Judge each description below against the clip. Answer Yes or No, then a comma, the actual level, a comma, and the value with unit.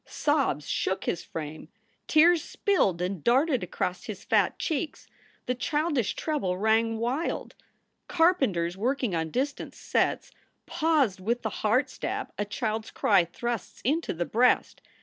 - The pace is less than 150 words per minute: Yes, average, 140 wpm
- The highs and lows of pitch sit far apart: Yes, wide, 7.4 semitones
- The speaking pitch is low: No, high, 235 Hz